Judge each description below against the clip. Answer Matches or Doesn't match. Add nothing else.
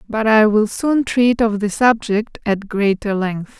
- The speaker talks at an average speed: Matches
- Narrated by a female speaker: Matches